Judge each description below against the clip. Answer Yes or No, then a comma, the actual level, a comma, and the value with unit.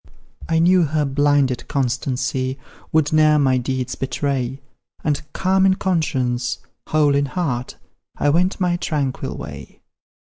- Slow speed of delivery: Yes, slow, 130 wpm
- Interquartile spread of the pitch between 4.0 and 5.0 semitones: No, average, 3.6 semitones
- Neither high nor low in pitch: Yes, medium, 145 Hz